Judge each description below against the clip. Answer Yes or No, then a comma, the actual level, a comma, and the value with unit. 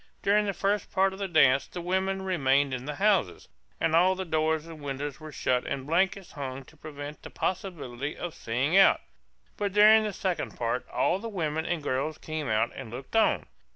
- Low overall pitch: No, medium, 160 Hz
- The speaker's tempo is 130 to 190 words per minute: No, average, 200 wpm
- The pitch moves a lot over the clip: Yes, wide, 5.7 semitones